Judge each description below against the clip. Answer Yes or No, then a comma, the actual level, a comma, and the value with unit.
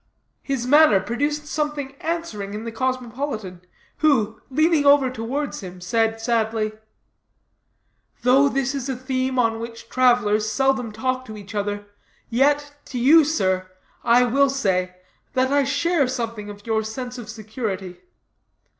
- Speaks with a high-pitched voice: Yes, high, 245 Hz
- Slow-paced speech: No, average, 145 wpm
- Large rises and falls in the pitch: No, average, 4.2 semitones